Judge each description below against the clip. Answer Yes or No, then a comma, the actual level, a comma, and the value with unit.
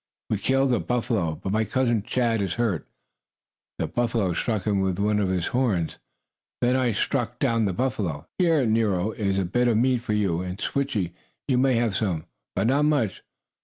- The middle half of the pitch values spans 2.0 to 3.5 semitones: No, average, 4.5 semitones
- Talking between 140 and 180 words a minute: No, average, 190 wpm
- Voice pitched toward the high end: No, low, 110 Hz